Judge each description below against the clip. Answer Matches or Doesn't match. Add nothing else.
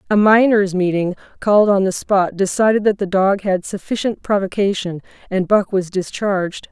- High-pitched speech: Matches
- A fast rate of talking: Doesn't match